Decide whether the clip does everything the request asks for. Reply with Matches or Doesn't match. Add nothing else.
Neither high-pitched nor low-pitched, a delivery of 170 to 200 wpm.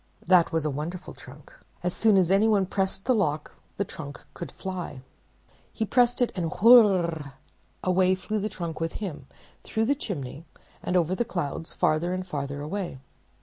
Matches